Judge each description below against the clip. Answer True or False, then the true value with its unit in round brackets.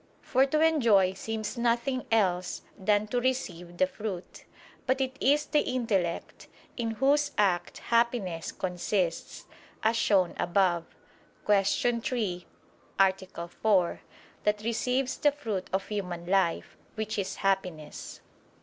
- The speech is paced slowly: True (120 wpm)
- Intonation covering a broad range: False (4.7 semitones)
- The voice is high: True (210 Hz)